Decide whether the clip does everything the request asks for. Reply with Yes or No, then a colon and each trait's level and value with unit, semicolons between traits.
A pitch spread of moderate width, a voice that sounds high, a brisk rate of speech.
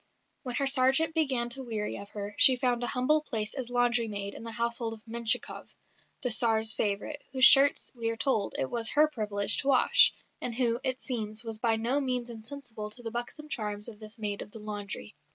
Yes: average, 3.0 semitones; high, 235 Hz; fast, 210 wpm